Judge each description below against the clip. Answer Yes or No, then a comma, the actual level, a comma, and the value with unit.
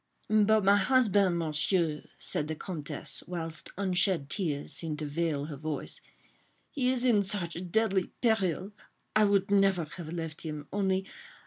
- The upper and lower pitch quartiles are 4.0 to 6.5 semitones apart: Yes, average, 4.3 semitones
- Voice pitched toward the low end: No, medium, 180 Hz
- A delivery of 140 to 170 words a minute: Yes, average, 145 wpm